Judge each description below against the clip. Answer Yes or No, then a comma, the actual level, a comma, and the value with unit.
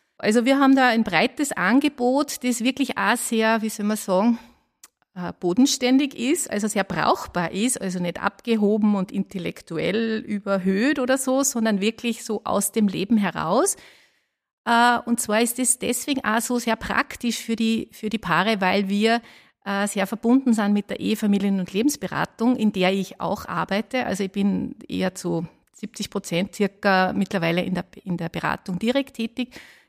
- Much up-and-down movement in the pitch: No, average, 3.6 semitones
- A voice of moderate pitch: No, high, 220 Hz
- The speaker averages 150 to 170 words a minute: Yes, average, 165 wpm